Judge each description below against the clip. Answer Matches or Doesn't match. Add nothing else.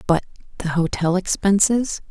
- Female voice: Matches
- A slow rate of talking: Matches